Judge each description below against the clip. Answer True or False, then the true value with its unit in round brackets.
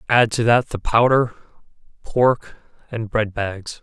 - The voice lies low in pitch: True (115 Hz)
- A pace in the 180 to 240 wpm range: False (140 wpm)